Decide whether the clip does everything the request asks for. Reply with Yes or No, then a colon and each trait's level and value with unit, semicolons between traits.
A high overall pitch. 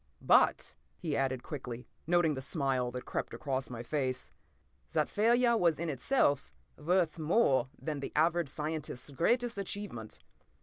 No: medium, 150 Hz